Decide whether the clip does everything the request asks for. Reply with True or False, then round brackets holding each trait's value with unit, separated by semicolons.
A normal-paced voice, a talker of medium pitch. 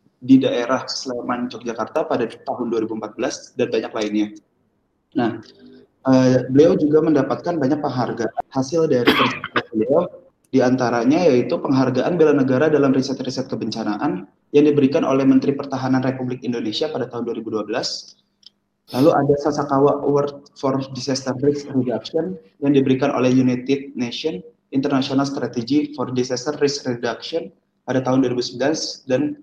False (125 wpm; 130 Hz)